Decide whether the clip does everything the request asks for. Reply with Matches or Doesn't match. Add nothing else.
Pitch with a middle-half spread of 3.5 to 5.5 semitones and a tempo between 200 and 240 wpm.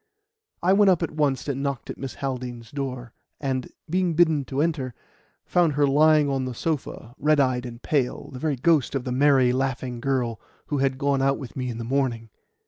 Doesn't match